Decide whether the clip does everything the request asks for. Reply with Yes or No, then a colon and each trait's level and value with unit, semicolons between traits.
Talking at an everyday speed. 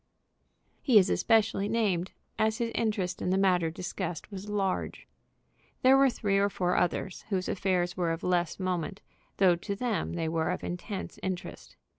Yes: average, 165 wpm